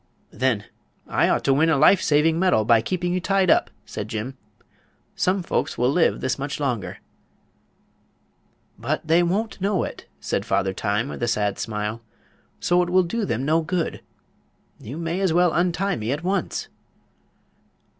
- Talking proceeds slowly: No, average, 165 wpm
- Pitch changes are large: Yes, wide, 7.2 semitones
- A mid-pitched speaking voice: Yes, medium, 160 Hz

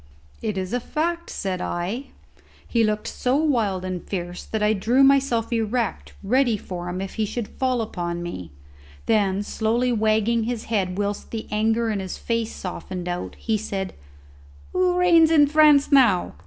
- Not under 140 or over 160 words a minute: No, average, 170 wpm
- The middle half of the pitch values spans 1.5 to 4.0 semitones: No, average, 4.6 semitones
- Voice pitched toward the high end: Yes, high, 220 Hz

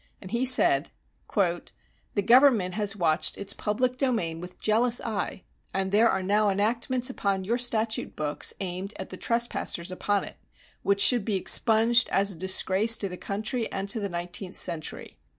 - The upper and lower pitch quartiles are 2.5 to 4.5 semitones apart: Yes, average, 3.7 semitones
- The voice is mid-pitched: No, high, 205 Hz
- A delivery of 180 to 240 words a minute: No, average, 165 wpm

